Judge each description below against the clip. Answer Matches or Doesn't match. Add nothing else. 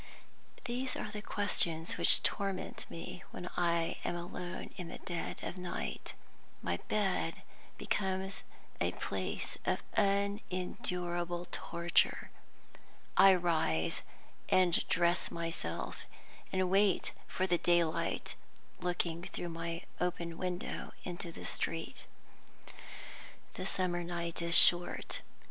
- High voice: Doesn't match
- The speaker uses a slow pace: Matches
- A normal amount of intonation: Doesn't match